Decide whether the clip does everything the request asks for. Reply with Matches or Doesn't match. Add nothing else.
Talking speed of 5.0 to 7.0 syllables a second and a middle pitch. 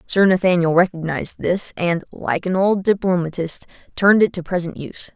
Matches